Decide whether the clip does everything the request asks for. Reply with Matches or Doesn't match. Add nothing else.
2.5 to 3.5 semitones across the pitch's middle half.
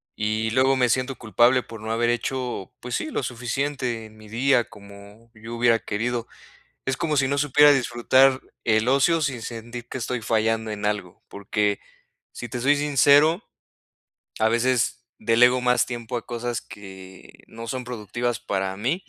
Matches